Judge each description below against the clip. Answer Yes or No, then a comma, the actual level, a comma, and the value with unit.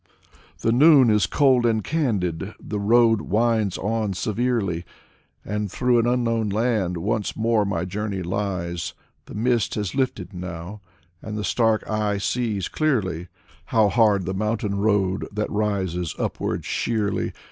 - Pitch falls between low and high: No, low, 105 Hz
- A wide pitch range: No, average, 3.1 semitones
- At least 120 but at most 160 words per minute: Yes, average, 140 wpm